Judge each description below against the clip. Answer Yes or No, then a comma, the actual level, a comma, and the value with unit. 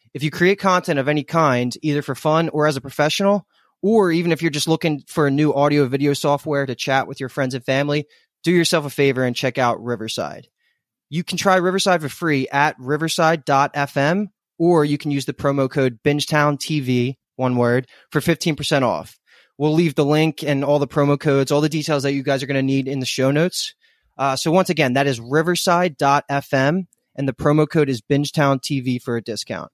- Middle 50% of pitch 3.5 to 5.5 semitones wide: No, average, 3.0 semitones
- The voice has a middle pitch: Yes, medium, 145 Hz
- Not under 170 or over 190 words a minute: No, fast, 205 wpm